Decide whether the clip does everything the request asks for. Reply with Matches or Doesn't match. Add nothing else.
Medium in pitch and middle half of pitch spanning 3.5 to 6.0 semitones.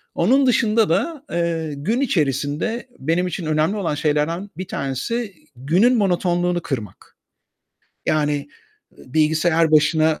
Matches